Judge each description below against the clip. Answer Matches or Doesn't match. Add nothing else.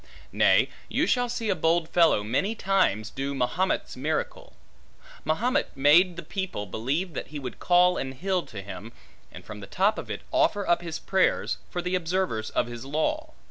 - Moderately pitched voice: Matches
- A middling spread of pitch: Doesn't match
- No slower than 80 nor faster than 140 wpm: Doesn't match